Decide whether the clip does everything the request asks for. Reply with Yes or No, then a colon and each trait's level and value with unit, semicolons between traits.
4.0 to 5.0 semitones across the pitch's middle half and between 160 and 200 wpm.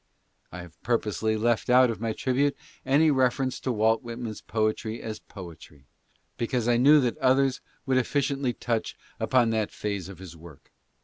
No: average, 3.2 semitones; average, 170 wpm